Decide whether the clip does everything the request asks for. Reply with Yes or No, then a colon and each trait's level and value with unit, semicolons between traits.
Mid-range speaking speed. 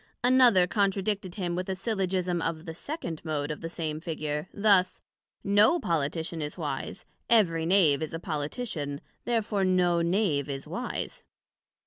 Yes: average, 145 wpm